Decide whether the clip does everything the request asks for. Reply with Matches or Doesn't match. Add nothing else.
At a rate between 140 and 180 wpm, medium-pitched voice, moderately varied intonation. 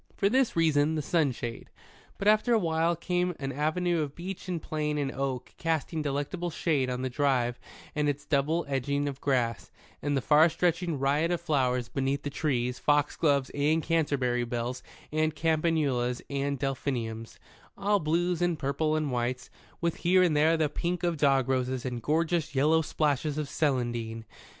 Matches